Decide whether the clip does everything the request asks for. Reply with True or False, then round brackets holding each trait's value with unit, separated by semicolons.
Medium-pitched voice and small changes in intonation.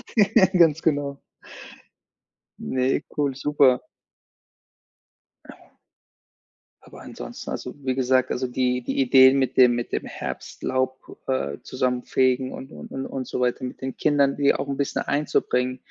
False (130 Hz; 1.7 semitones)